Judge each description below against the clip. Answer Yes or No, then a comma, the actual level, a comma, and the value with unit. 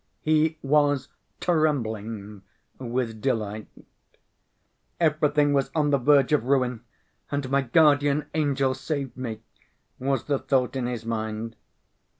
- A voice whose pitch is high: No, low, 135 Hz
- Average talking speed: No, slow, 120 wpm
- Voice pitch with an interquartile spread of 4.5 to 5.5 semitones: No, average, 4.0 semitones